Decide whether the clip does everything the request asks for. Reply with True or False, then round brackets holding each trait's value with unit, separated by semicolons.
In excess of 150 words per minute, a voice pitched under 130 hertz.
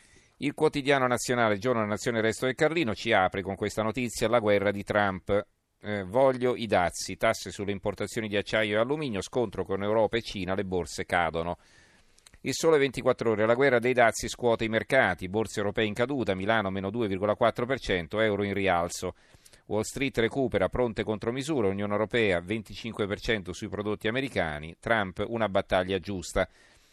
True (165 wpm; 110 Hz)